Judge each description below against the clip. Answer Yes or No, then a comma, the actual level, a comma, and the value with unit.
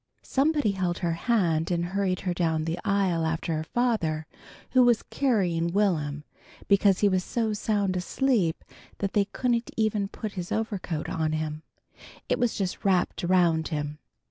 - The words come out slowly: No, average, 160 wpm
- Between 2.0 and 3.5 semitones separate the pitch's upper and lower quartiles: No, average, 4.4 semitones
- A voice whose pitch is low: No, medium, 185 Hz